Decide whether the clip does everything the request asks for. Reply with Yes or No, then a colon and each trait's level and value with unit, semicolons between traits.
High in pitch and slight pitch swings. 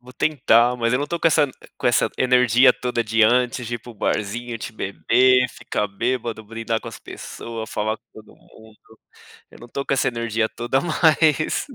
No: low, 120 Hz; narrow, 2.2 semitones